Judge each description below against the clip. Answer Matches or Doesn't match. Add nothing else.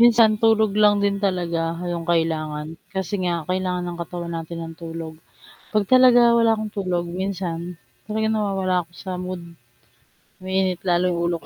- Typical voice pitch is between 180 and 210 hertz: Matches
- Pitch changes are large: Doesn't match